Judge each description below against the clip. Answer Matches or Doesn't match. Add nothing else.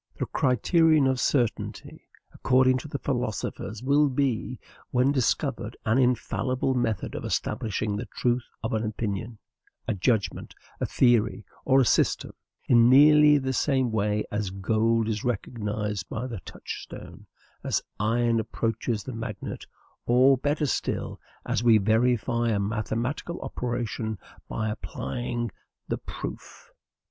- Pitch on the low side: Matches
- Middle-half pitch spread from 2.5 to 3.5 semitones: Matches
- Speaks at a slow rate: Matches